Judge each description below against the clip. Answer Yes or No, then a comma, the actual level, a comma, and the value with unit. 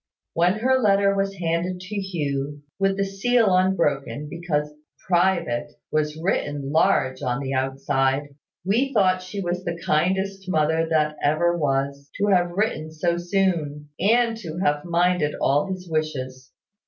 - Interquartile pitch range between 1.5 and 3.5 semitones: No, average, 4.6 semitones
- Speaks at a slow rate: No, average, 145 wpm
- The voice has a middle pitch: Yes, medium, 170 Hz